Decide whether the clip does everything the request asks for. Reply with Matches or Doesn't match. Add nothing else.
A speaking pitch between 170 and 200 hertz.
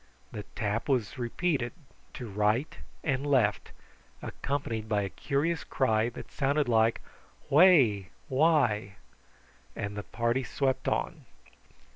Doesn't match